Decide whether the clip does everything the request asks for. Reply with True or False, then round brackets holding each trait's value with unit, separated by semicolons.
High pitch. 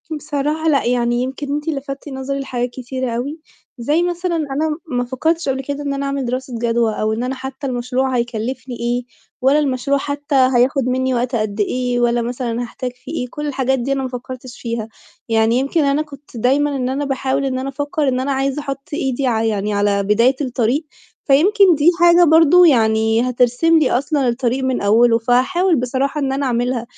True (260 Hz)